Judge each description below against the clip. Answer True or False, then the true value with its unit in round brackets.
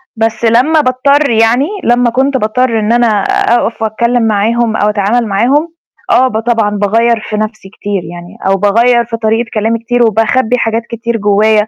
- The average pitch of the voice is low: False (230 Hz)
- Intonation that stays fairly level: True (2.0 semitones)